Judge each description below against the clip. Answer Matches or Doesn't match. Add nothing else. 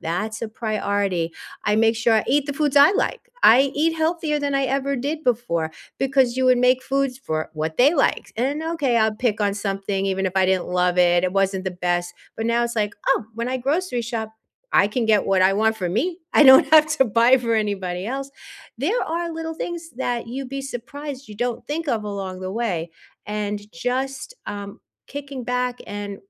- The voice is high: Matches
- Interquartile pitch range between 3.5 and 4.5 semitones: Doesn't match